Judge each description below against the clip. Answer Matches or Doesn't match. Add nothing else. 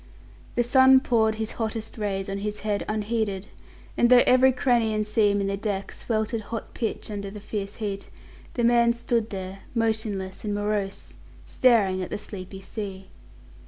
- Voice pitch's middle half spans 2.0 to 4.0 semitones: Matches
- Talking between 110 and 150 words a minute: Doesn't match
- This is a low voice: Doesn't match